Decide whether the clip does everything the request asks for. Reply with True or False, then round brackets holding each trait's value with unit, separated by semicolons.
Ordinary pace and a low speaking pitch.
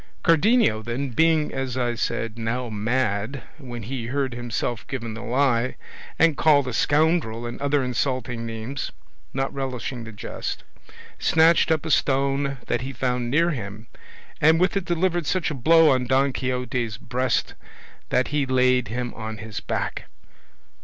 True (155 wpm; 130 Hz)